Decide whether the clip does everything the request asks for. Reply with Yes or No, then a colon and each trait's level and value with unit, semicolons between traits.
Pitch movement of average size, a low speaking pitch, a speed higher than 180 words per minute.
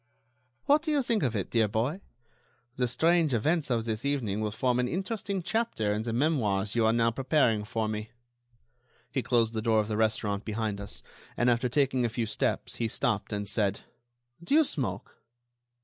Yes: average, 4.8 semitones; low, 115 Hz; average, 190 wpm